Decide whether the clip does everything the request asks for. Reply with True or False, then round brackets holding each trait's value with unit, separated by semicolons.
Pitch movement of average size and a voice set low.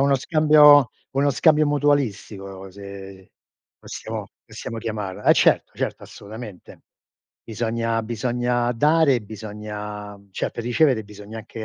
True (4.8 semitones; 115 Hz)